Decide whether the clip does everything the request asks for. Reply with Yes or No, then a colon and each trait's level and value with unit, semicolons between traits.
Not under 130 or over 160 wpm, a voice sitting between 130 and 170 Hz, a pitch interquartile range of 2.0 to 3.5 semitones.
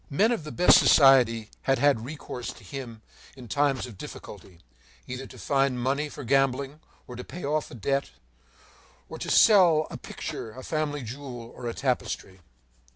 No: average, 170 wpm; low, 135 Hz; average, 3.1 semitones